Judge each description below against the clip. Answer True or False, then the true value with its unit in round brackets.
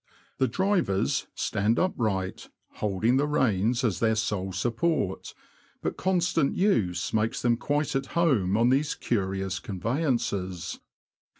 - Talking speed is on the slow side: True (120 wpm)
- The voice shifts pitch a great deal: True (6.7 semitones)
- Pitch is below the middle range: True (115 Hz)